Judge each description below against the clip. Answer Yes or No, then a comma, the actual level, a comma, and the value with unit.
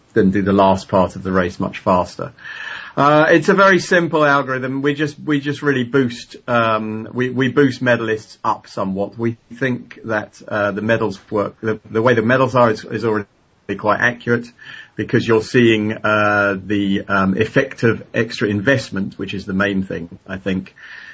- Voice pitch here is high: No, low, 110 Hz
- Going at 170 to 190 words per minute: Yes, average, 180 wpm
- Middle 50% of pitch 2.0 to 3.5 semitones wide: No, average, 4.3 semitones